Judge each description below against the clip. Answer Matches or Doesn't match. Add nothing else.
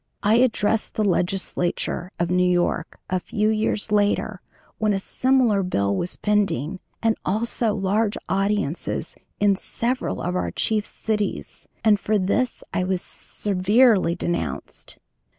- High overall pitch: Matches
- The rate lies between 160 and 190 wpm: Doesn't match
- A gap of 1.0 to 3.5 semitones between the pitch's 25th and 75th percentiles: Matches